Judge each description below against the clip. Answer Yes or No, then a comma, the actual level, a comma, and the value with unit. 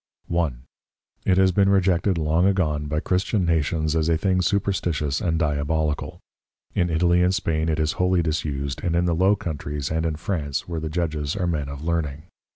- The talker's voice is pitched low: Yes, very low, 80 Hz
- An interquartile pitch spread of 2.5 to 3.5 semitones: Yes, average, 2.8 semitones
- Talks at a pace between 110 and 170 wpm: No, average, 185 wpm